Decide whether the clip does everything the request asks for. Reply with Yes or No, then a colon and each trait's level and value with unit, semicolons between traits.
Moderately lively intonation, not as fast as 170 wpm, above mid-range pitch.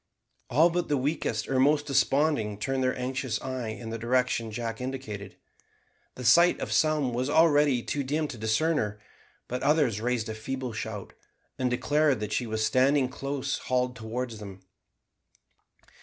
No: average, 4.1 semitones; average, 160 wpm; low, 130 Hz